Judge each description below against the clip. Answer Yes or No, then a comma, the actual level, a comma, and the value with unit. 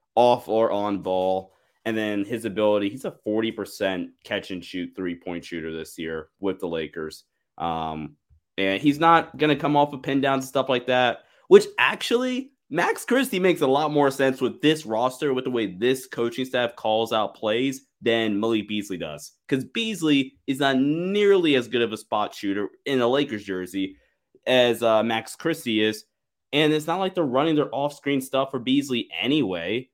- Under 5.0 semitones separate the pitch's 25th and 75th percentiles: No, wide, 5.6 semitones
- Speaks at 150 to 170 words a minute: No, average, 190 wpm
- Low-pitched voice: Yes, low, 125 Hz